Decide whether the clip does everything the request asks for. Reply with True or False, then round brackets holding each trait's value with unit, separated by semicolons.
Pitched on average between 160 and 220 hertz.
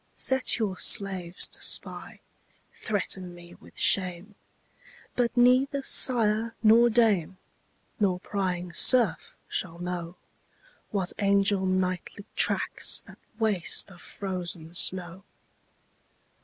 True (190 Hz)